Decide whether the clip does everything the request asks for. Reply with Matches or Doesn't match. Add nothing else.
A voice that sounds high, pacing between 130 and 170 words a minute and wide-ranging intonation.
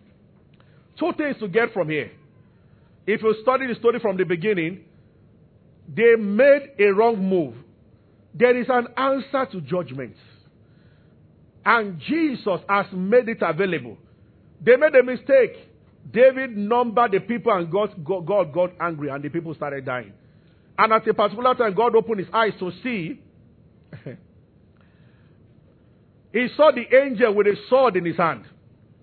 Matches